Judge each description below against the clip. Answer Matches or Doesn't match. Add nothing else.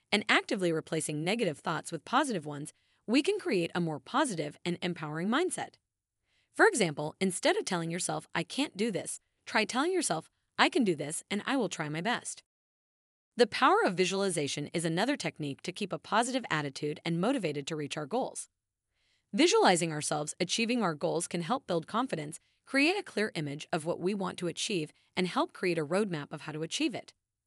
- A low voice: Doesn't match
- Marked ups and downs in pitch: Matches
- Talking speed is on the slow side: Doesn't match